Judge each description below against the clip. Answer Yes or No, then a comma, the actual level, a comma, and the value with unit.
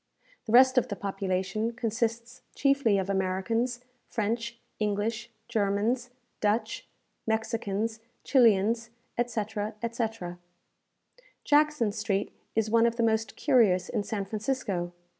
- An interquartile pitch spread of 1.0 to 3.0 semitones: Yes, narrow, 2.5 semitones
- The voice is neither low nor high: No, high, 225 Hz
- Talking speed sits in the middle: No, slow, 110 wpm